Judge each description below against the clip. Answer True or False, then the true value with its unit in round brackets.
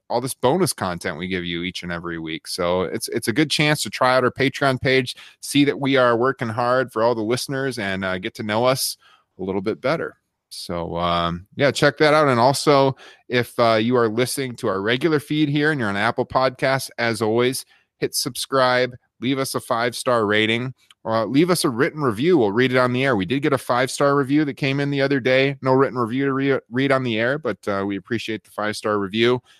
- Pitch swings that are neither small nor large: True (3.2 semitones)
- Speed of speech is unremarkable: False (240 wpm)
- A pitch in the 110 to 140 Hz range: True (125 Hz)